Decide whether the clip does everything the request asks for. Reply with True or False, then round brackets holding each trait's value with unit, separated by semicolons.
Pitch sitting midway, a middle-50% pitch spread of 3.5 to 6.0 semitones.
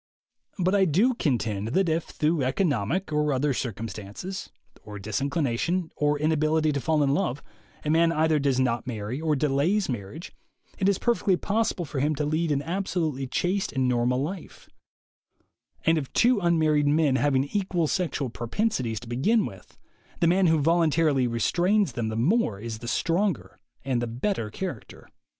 True (150 Hz; 5.4 semitones)